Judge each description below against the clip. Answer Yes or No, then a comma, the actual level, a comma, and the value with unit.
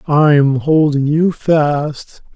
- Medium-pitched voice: Yes, medium, 150 Hz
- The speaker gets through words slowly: Yes, slow, 125 wpm